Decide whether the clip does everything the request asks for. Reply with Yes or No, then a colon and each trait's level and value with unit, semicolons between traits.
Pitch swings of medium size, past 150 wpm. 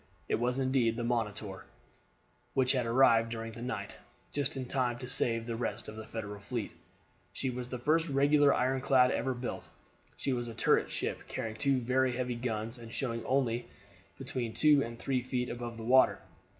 No: narrow, 2.2 semitones; average, 185 wpm